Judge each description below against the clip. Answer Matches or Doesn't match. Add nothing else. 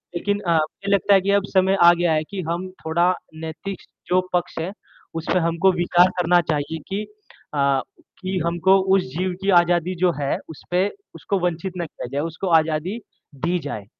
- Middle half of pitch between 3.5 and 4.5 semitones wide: Doesn't match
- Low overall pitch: Doesn't match